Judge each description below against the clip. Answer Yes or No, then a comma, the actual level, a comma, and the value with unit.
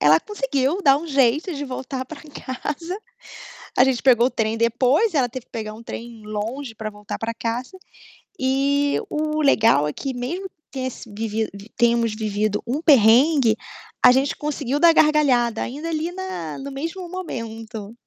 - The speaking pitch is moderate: No, very high, 260 Hz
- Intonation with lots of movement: No, average, 4.8 semitones